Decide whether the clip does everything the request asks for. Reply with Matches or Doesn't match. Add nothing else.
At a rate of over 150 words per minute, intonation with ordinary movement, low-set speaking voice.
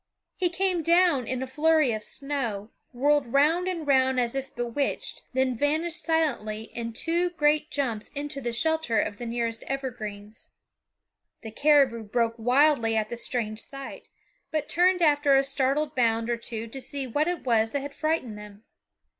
Doesn't match